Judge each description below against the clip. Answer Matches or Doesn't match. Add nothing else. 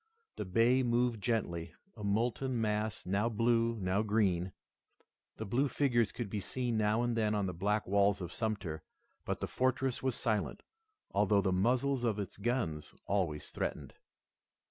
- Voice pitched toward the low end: Matches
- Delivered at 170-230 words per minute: Doesn't match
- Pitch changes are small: Doesn't match